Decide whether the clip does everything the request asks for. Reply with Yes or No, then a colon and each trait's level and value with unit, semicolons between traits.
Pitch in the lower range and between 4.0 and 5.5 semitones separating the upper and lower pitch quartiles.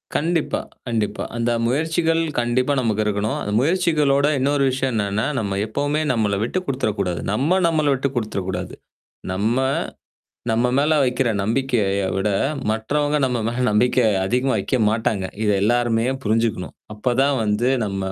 Yes: low, 120 Hz; average, 4.6 semitones